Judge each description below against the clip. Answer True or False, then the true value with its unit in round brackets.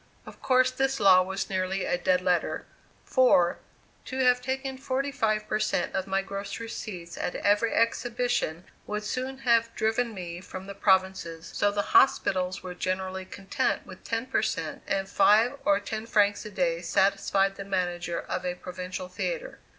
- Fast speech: False (170 wpm)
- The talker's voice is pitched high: True (200 Hz)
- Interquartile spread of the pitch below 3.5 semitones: False (3.8 semitones)